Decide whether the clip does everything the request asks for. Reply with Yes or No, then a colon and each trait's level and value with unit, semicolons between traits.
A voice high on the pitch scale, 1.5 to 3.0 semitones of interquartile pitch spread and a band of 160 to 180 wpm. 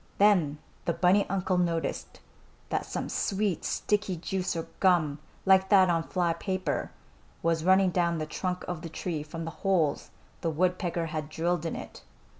No: medium, 175 Hz; narrow, 2.4 semitones; average, 165 wpm